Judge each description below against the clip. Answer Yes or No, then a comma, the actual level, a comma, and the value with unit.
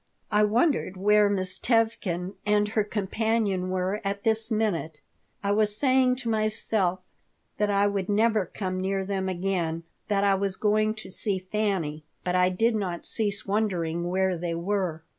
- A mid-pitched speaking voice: No, high, 200 Hz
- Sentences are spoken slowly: No, average, 160 wpm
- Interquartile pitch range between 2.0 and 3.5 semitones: Yes, narrow, 2.6 semitones